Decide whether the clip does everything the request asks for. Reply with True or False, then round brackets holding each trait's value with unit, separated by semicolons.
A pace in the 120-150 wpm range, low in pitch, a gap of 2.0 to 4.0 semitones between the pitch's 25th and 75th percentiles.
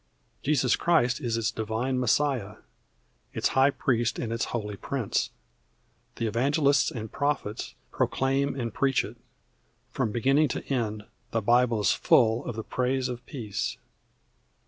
True (140 wpm; 120 Hz; 3.2 semitones)